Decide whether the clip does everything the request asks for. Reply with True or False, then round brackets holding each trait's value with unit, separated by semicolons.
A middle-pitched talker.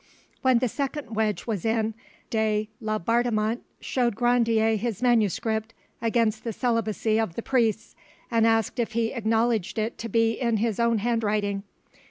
False (225 Hz)